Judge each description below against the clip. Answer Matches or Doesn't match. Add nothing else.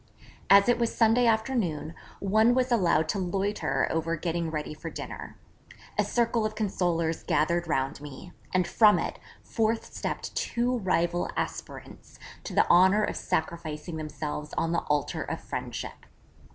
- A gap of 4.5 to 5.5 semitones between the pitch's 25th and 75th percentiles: Matches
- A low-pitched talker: Doesn't match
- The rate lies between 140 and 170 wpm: Matches